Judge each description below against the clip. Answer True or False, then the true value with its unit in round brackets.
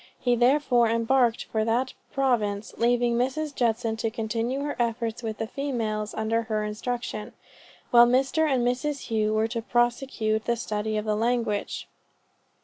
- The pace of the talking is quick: False (150 wpm)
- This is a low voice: False (235 Hz)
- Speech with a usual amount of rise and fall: False (2.2 semitones)